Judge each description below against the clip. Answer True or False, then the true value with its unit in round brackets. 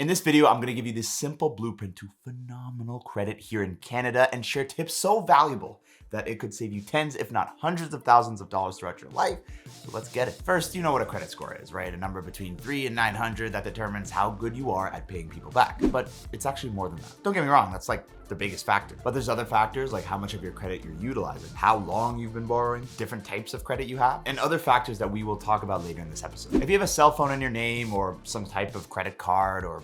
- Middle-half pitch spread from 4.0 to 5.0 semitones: True (4.3 semitones)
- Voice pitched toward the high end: False (115 Hz)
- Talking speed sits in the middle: False (265 wpm)